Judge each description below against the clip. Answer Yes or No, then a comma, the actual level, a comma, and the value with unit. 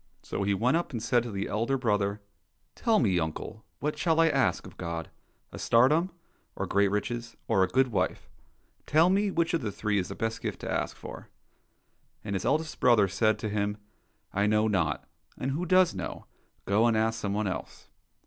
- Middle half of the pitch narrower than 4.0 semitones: No, average, 5.2 semitones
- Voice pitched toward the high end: No, low, 110 Hz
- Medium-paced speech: No, fast, 215 wpm